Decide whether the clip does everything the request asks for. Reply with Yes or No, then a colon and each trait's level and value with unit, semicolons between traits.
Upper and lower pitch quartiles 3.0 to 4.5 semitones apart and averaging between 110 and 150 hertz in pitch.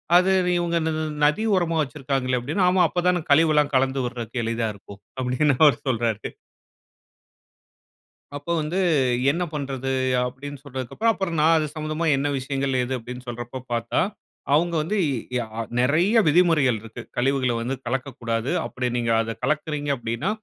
Yes: average, 4.2 semitones; low, 135 Hz